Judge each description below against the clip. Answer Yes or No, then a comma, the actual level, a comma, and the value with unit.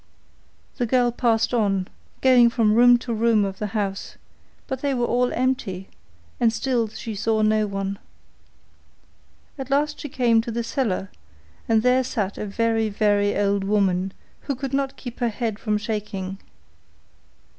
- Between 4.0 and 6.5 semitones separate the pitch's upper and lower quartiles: No, average, 3.2 semitones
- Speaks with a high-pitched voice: Yes, high, 225 Hz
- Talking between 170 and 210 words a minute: No, average, 155 wpm